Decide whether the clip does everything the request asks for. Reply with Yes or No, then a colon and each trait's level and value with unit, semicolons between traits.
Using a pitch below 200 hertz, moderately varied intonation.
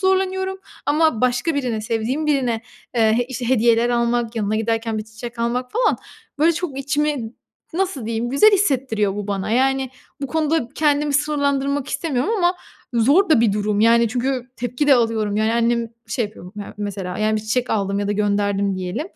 No: high, 240 Hz; average, 4.6 semitones